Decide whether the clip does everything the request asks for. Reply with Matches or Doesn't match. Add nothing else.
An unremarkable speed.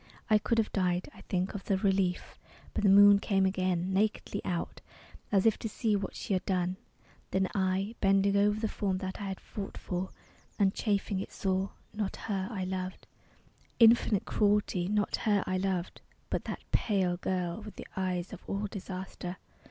Matches